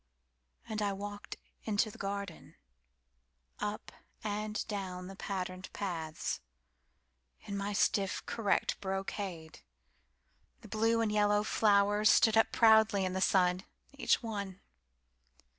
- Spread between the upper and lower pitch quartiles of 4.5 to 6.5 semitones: No, average, 3.4 semitones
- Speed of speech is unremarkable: No, slow, 100 wpm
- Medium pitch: No, high, 200 Hz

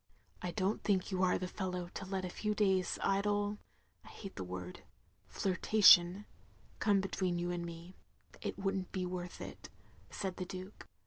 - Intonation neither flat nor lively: No, narrow, 1.8 semitones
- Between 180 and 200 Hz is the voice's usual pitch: Yes, medium, 185 Hz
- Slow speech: No, average, 195 wpm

